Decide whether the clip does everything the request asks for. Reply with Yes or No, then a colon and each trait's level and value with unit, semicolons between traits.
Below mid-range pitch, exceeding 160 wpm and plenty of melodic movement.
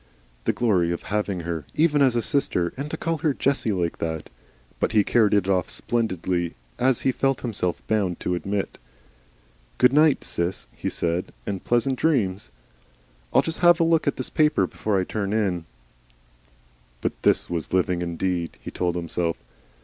Yes: low, 100 Hz; average, 170 wpm; wide, 7.2 semitones